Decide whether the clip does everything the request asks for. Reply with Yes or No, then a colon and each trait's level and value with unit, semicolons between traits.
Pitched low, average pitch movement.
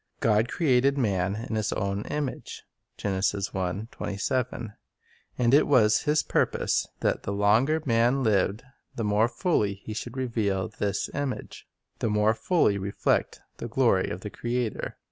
Yes: low, 110 Hz; average, 3.8 semitones